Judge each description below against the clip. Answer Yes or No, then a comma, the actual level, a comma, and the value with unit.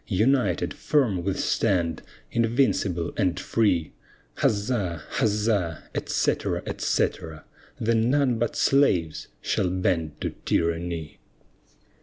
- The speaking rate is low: Yes, slow, 95 wpm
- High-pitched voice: No, very low, 95 Hz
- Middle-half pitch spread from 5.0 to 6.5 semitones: Yes, wide, 5.4 semitones